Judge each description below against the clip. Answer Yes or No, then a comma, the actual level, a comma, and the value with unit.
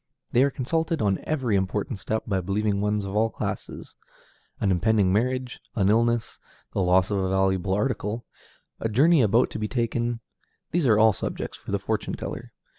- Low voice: Yes, low, 110 Hz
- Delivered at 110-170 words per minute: No, average, 180 wpm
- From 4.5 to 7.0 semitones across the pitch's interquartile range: No, average, 3.5 semitones